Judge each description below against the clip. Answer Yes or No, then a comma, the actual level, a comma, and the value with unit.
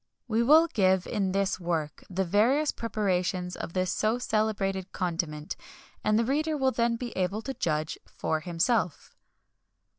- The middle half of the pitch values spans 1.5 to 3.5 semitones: No, average, 4.6 semitones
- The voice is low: No, high, 195 Hz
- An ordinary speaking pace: Yes, average, 150 wpm